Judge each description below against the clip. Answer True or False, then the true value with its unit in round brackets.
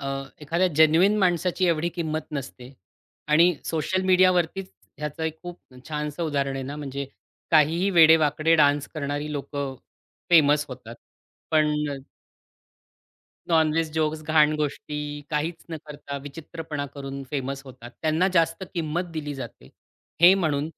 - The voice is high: False (155 Hz)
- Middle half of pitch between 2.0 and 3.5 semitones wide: True (2.4 semitones)